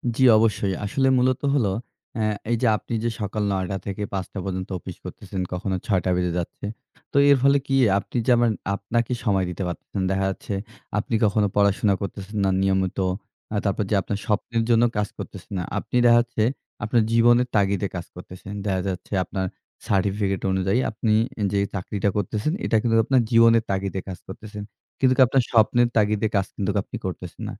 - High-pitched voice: No, low, 105 Hz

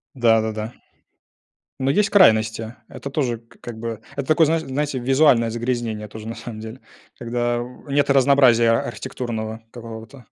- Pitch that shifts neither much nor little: Yes, average, 3.1 semitones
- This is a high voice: No, low, 120 Hz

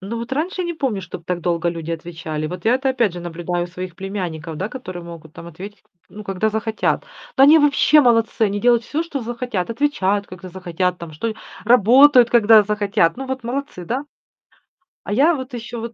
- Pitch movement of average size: No, wide, 6.1 semitones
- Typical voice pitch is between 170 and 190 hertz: No, high, 210 Hz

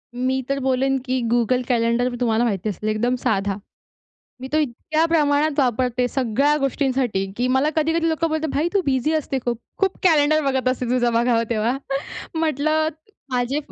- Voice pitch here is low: No, very high, 260 Hz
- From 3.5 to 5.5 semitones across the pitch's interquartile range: Yes, average, 3.8 semitones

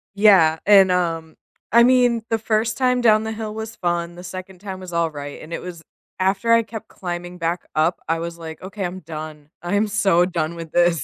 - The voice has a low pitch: No, medium, 180 Hz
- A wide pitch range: No, average, 4.3 semitones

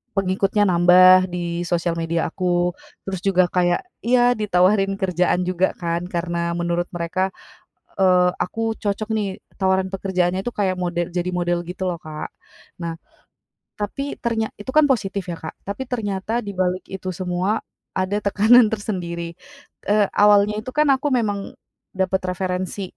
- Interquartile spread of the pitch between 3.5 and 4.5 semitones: No, average, 2.7 semitones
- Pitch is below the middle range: No, medium, 185 Hz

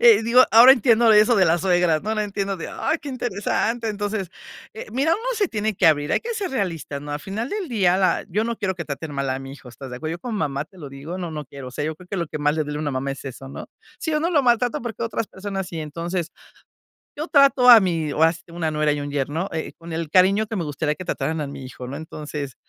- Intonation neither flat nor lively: No, wide, 6.8 semitones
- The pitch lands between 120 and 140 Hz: No, medium, 175 Hz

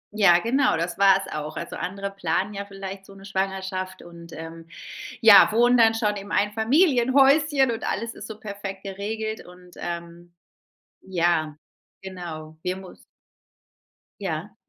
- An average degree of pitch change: Yes, average, 3.9 semitones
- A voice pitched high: Yes, high, 195 Hz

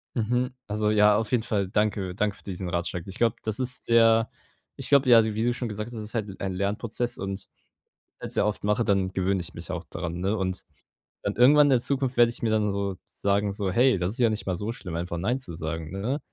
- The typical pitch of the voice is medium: No, low, 105 Hz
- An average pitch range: Yes, average, 3.5 semitones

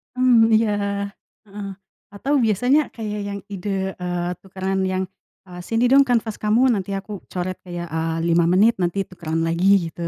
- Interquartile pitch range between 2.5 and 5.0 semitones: Yes, average, 3.8 semitones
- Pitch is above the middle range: Yes, high, 195 Hz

